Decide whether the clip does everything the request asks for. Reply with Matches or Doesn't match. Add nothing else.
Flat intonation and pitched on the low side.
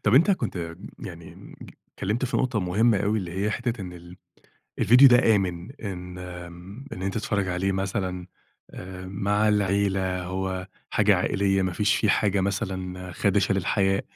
Matches